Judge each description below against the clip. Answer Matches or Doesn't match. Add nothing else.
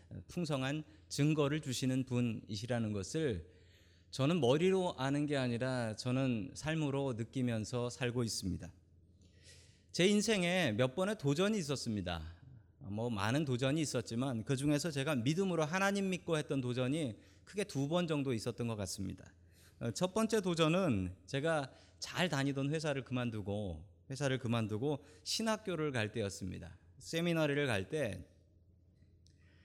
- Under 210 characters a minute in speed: Doesn't match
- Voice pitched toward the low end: Matches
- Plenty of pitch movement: Matches